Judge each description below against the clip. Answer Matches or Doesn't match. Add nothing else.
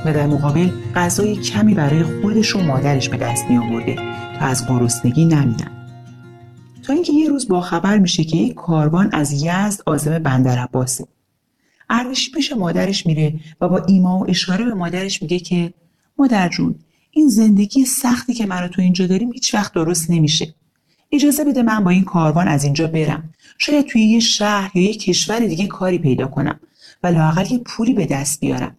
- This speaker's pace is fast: Matches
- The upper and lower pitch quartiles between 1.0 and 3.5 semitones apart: Doesn't match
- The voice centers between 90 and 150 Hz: Doesn't match